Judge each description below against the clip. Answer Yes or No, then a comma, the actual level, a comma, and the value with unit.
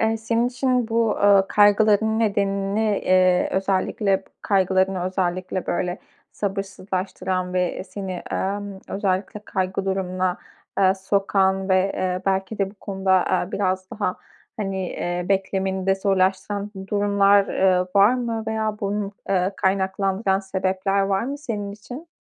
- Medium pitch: No, high, 195 Hz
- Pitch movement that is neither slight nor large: No, narrow, 1.5 semitones